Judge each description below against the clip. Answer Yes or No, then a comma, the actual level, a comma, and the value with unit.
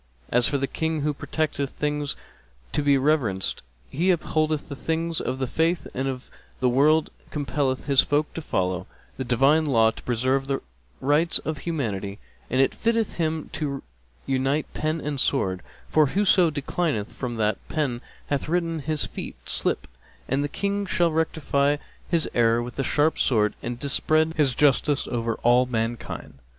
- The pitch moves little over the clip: No, average, 3.9 semitones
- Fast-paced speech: No, average, 170 wpm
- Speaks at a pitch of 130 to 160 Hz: Yes, medium, 140 Hz